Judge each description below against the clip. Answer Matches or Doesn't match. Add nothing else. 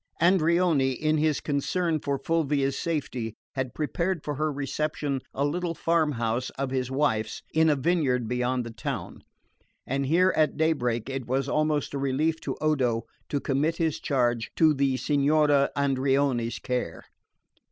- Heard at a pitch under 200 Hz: Matches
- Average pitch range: Matches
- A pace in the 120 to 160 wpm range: Matches